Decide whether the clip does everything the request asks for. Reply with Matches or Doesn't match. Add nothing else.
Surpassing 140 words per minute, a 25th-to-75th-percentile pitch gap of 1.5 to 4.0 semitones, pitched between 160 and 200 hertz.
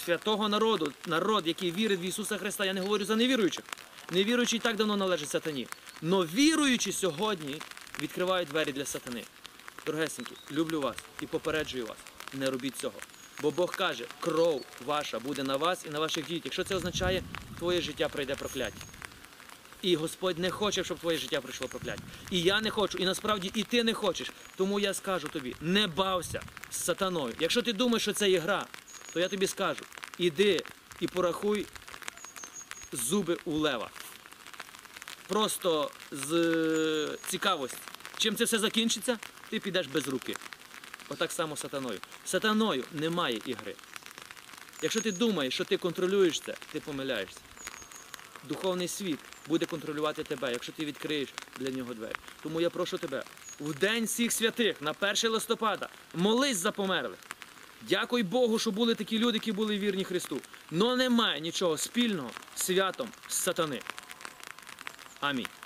Doesn't match